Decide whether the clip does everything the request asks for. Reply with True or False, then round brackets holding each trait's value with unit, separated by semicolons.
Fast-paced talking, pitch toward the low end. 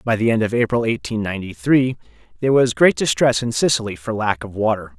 True (215 wpm; 115 Hz)